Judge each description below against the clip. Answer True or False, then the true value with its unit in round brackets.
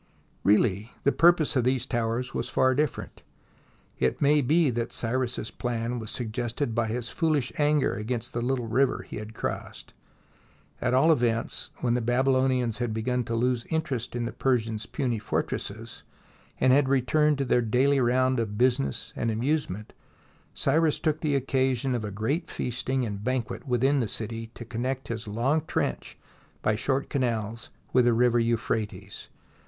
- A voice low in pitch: True (125 Hz)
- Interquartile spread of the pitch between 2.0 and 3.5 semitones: True (2.8 semitones)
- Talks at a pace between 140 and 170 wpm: True (160 wpm)